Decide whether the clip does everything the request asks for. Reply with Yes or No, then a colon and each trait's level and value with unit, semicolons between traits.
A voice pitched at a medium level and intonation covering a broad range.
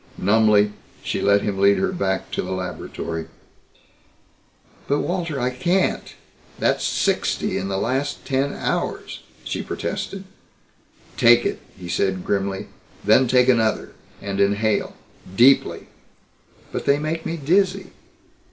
No: low, 110 Hz; wide, 6.6 semitones